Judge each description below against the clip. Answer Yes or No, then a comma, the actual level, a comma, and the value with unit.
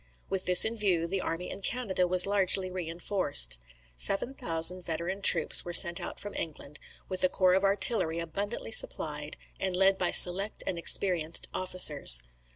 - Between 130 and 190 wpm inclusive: Yes, average, 160 wpm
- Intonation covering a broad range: No, average, 2.8 semitones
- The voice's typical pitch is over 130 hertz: Yes, medium, 185 Hz